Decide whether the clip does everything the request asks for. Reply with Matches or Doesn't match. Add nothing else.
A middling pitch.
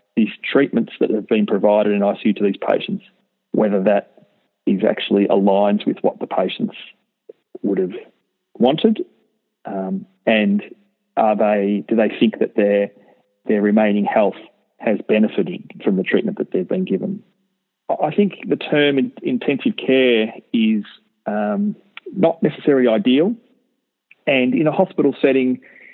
Doesn't match